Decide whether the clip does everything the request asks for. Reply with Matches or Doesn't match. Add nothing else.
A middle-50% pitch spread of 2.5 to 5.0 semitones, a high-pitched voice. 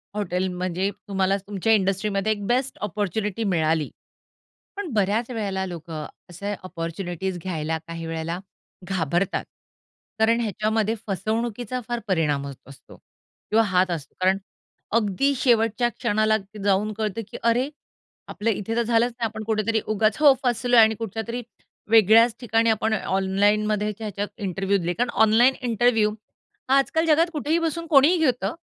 Matches